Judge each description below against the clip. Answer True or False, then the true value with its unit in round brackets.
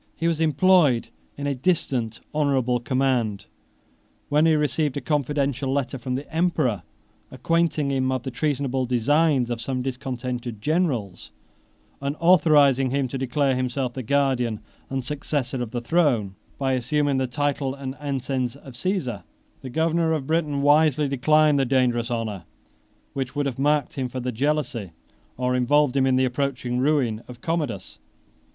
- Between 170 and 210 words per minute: False (160 wpm)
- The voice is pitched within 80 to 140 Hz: True (135 Hz)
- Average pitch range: True (3.0 semitones)